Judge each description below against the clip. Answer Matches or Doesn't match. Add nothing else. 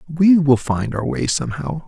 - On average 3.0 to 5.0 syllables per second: Matches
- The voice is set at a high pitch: Doesn't match